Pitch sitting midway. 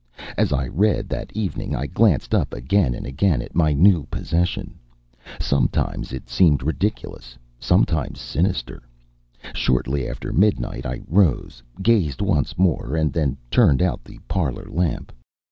No: very low, 75 Hz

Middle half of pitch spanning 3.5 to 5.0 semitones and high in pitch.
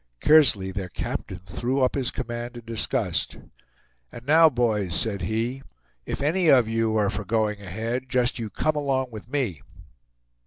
No: average, 3.8 semitones; low, 120 Hz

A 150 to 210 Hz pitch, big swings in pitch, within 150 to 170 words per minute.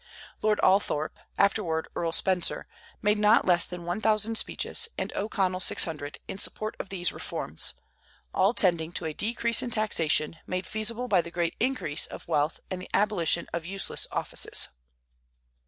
No: high, 190 Hz; average, 4.1 semitones; average, 160 wpm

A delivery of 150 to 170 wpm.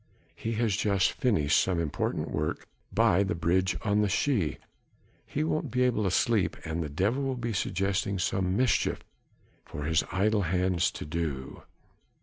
Yes: average, 160 wpm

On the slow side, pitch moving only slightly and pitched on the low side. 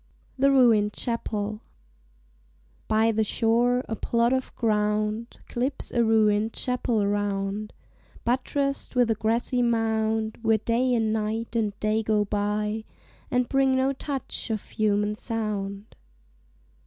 No: slow, 125 wpm; narrow, 2.3 semitones; high, 220 Hz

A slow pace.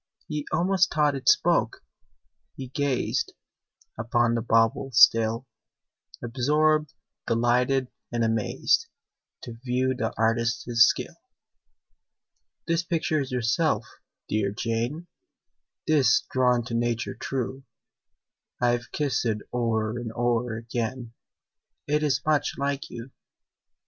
Yes: slow, 110 wpm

